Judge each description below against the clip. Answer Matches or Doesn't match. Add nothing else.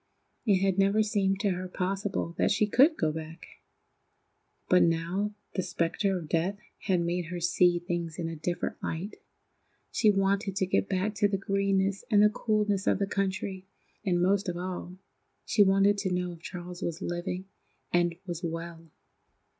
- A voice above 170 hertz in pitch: Matches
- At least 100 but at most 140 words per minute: Doesn't match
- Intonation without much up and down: Matches